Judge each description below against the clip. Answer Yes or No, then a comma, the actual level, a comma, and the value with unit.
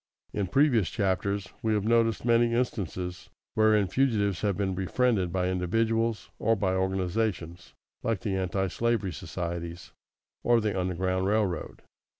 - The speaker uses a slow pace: Yes, slow, 130 wpm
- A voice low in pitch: Yes, low, 100 Hz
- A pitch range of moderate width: Yes, average, 3.6 semitones